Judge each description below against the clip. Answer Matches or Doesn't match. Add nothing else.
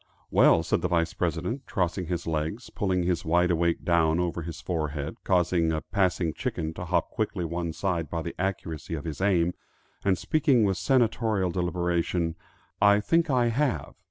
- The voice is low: Matches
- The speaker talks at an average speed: Matches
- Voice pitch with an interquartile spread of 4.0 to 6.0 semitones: Doesn't match